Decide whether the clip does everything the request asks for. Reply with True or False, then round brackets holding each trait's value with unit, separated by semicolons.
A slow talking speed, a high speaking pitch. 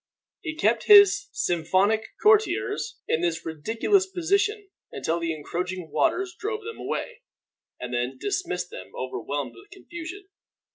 True (130 wpm; 205 Hz)